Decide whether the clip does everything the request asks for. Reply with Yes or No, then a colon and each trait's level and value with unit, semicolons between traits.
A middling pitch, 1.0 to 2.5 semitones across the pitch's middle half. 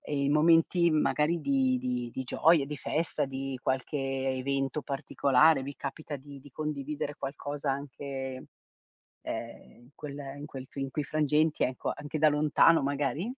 Yes: medium, 145 Hz; narrow, 2.2 semitones